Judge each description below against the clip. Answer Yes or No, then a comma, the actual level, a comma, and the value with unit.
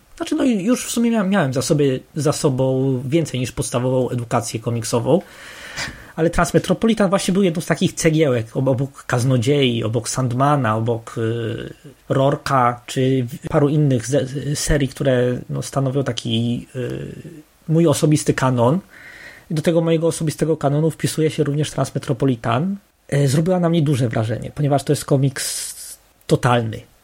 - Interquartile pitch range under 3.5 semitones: No, average, 4.3 semitones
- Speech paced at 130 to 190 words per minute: Yes, average, 135 wpm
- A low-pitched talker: No, medium, 145 Hz